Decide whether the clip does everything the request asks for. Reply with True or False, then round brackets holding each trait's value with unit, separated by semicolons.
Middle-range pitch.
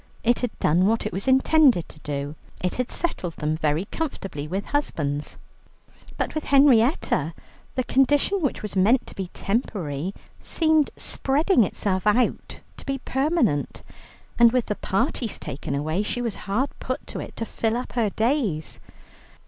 False (225 Hz)